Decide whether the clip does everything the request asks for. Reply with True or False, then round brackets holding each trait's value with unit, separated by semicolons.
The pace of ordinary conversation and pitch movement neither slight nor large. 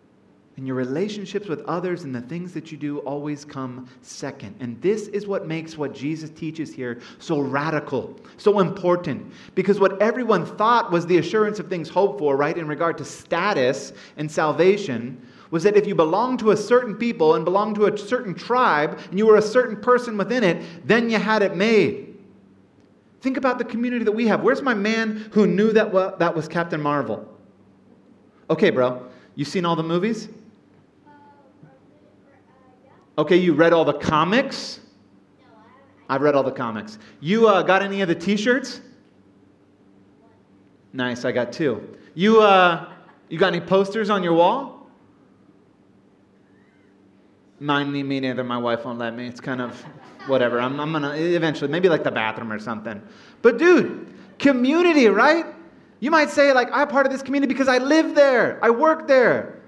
False (170 wpm; 8.0 semitones)